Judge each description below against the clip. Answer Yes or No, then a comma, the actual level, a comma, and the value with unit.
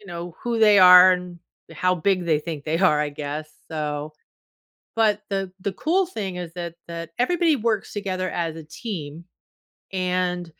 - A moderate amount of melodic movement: Yes, average, 3.6 semitones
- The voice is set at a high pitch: No, medium, 180 Hz